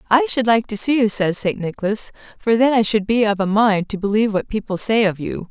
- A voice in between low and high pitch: No, high, 215 Hz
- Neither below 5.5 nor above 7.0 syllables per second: Yes, 5.7 syllables/s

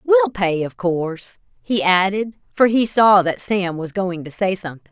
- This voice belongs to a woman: Yes, female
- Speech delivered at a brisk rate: No, average, 195 wpm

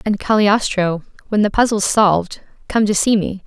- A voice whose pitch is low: No, high, 205 Hz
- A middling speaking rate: Yes, average, 175 wpm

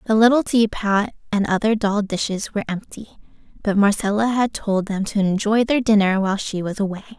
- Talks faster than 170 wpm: Yes, average, 185 wpm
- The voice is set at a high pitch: Yes, high, 205 Hz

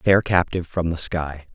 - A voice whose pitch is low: Yes, very low, 85 Hz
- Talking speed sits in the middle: No, fast, 235 wpm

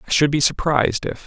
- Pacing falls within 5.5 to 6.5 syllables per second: Yes, 6.3 syllables/s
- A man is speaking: Yes, male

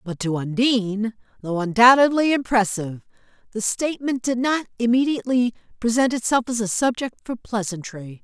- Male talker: No, female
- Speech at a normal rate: No, slow, 130 wpm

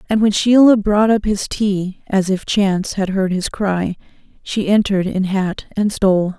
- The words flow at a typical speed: Yes, average, 190 wpm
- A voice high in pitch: Yes, high, 200 Hz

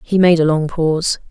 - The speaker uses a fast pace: Yes, fast, 230 wpm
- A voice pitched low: No, medium, 165 Hz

